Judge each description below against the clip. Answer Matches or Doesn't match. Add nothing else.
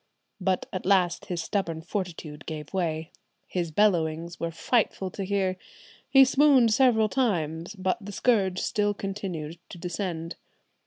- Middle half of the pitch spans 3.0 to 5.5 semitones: Matches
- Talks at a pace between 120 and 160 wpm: Matches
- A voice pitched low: Doesn't match